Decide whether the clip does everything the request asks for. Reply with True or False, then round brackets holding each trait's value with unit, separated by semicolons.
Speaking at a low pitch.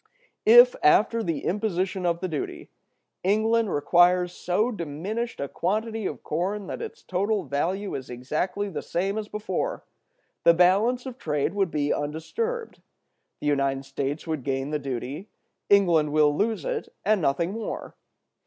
False (180 Hz)